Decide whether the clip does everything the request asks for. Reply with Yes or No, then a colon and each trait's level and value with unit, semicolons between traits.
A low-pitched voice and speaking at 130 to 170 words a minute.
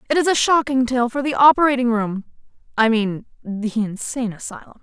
No: high, 240 Hz; average, 160 wpm